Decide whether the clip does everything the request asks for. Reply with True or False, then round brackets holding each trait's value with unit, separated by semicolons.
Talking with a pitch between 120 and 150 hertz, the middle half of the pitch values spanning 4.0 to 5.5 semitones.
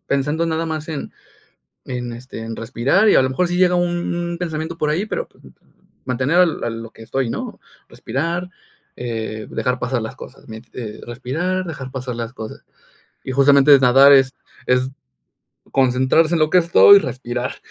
True (135 Hz; 5.1 semitones)